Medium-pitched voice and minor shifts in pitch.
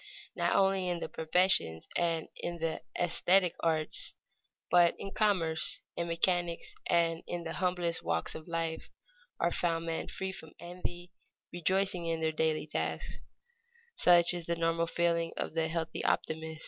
Yes: medium, 170 Hz; narrow, 1.4 semitones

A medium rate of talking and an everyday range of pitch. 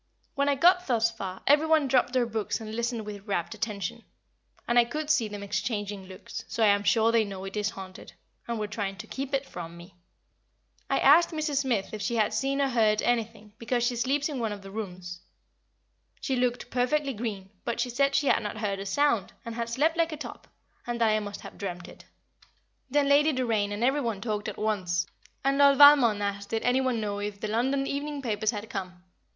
No: fast, 220 wpm; average, 4.8 semitones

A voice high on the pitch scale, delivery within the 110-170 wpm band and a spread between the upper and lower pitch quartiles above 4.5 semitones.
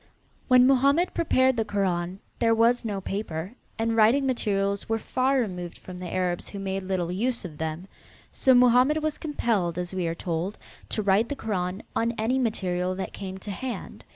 No: high, 205 Hz; average, 180 wpm; average, 5.2 semitones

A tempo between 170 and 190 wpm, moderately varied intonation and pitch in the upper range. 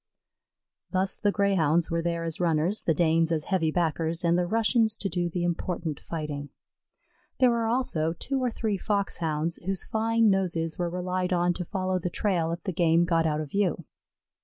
No: average, 185 wpm; average, 3.1 semitones; medium, 175 Hz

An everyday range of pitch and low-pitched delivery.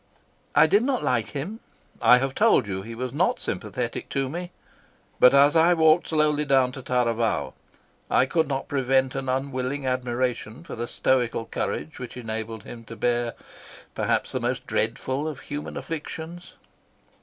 Yes: average, 4.0 semitones; low, 130 Hz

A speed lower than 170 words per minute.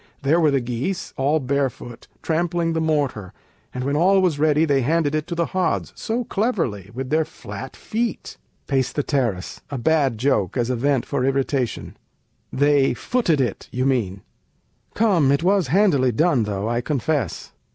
Yes: average, 160 wpm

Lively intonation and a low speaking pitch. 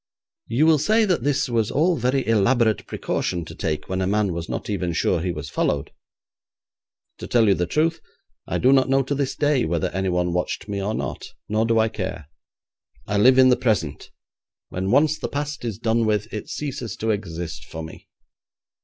Yes: wide, 6.3 semitones; low, 110 Hz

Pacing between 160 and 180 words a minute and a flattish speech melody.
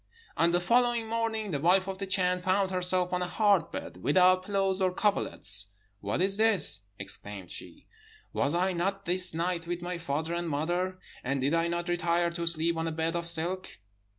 No: average, 195 wpm; narrow, 2.3 semitones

